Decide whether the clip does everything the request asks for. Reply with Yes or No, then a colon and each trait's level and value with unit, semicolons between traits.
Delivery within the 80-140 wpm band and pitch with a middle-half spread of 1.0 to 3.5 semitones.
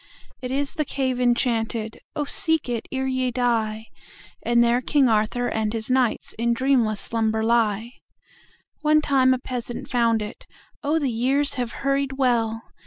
Yes: slow, 135 wpm; average, 2.8 semitones